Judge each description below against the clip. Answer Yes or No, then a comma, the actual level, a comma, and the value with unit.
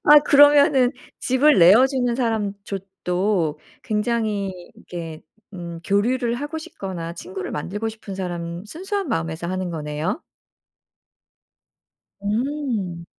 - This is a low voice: No, high, 205 Hz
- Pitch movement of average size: No, wide, 6.6 semitones